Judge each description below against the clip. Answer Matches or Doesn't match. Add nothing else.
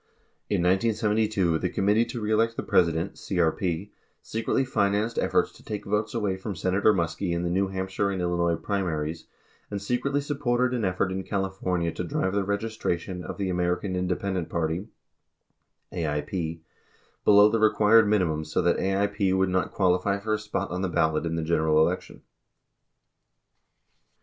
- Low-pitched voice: Matches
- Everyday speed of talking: Matches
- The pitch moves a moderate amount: Matches